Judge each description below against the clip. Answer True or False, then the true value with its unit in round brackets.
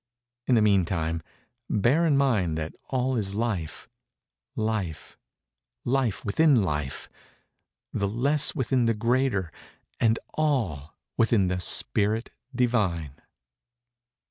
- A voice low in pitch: True (110 Hz)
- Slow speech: True (90 wpm)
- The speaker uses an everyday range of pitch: False (6.0 semitones)